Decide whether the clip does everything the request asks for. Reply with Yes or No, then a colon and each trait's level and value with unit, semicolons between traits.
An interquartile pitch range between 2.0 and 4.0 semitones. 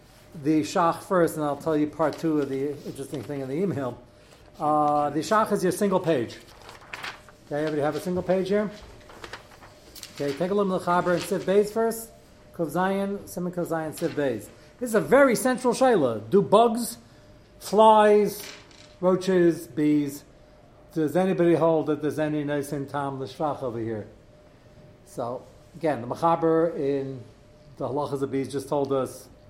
No: average, 4.8 semitones